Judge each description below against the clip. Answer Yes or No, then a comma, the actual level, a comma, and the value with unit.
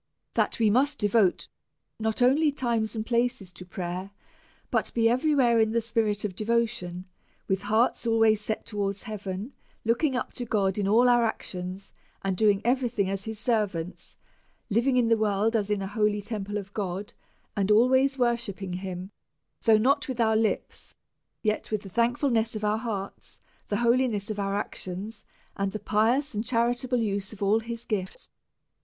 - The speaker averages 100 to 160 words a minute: No, average, 175 wpm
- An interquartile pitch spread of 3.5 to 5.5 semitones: No, average, 2.9 semitones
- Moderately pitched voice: No, high, 220 Hz